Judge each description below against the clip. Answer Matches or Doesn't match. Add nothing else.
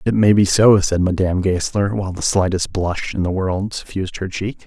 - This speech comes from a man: Matches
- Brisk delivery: Matches